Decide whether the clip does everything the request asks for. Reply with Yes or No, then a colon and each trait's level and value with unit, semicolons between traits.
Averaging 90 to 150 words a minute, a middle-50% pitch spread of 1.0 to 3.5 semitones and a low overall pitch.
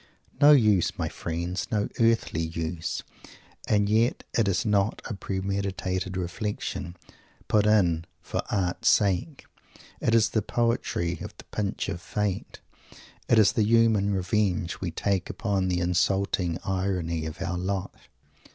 Yes: average, 140 wpm; average, 3.1 semitones; very low, 95 Hz